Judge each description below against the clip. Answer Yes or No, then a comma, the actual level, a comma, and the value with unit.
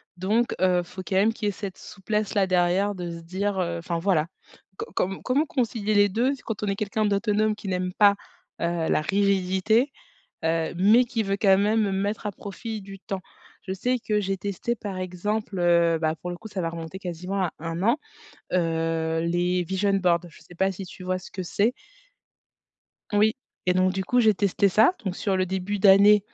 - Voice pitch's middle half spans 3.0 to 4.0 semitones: No, narrow, 2.6 semitones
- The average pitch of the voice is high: Yes, high, 195 Hz